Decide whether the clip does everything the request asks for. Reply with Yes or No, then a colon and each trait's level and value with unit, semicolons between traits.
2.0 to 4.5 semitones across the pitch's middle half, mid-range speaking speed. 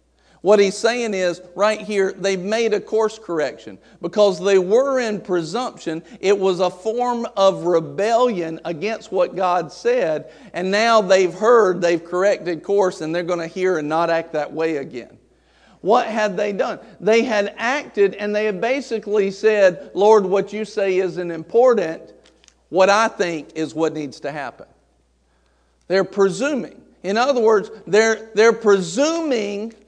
Yes: average, 3.9 semitones; average, 155 wpm